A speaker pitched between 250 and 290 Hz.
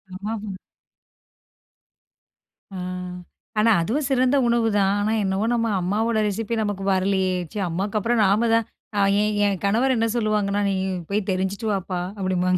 No: high, 205 Hz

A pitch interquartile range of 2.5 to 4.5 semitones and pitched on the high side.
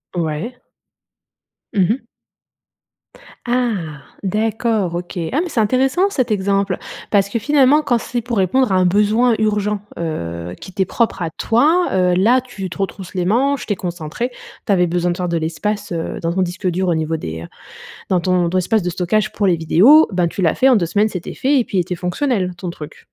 No: average, 5.0 semitones; high, 195 Hz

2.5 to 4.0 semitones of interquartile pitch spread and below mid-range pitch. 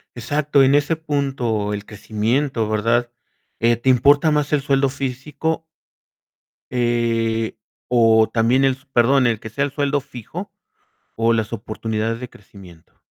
Yes: average, 3.7 semitones; low, 120 Hz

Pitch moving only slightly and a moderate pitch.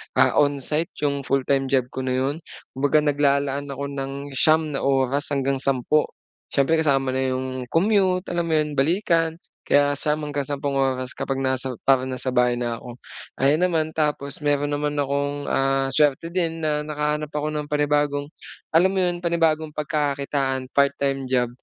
Yes: narrow, 2.1 semitones; medium, 145 Hz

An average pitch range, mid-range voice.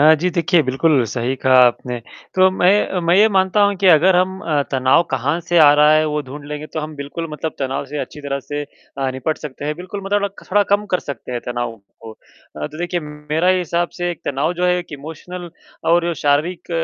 Yes: average, 3.8 semitones; medium, 155 Hz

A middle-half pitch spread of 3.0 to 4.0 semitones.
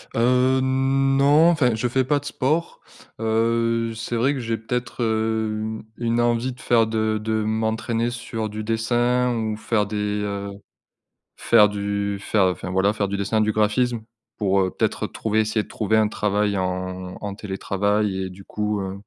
No: narrow, 2.5 semitones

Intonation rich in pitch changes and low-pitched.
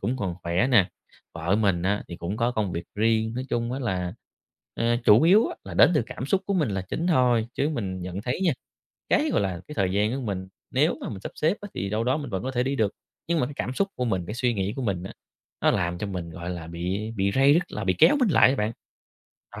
Yes: wide, 5.7 semitones; low, 110 Hz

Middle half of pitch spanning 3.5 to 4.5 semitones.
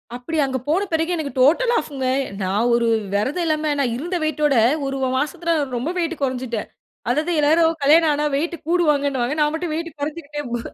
Yes: average, 3.8 semitones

